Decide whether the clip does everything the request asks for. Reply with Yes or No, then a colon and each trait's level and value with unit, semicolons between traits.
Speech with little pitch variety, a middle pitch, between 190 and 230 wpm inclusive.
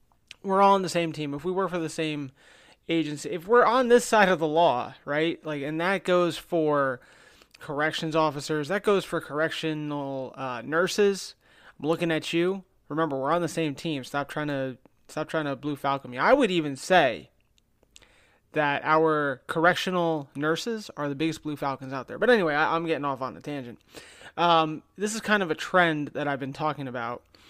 No: average, 3.4 semitones; medium, 155 Hz; average, 195 wpm